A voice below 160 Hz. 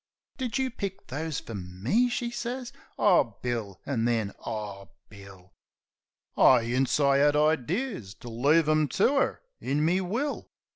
Yes: medium, 140 Hz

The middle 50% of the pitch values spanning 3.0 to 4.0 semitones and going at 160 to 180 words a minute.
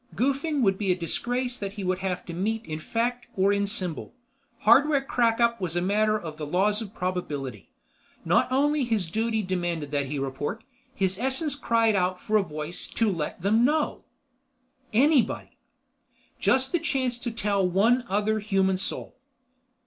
No: average, 4.8 semitones; average, 165 wpm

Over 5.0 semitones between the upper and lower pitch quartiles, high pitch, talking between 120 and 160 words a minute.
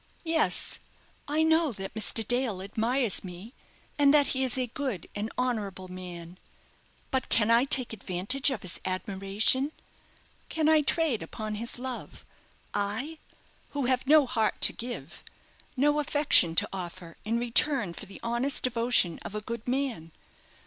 Yes: wide, 5.4 semitones; high, 235 Hz; average, 150 wpm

